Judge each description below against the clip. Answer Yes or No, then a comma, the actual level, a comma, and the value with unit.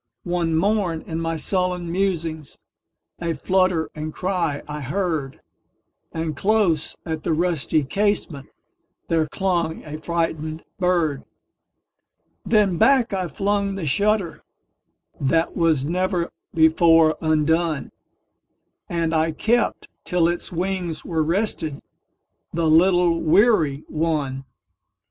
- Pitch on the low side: No, medium, 165 Hz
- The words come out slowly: Yes, slow, 95 wpm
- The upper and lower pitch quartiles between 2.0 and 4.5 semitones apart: Yes, average, 2.7 semitones